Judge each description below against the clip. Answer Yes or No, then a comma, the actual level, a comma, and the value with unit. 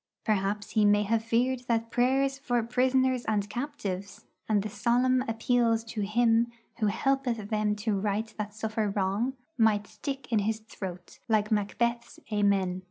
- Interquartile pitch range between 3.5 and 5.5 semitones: No, average, 2.7 semitones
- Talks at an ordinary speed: Yes, average, 155 wpm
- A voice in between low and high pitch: No, high, 220 Hz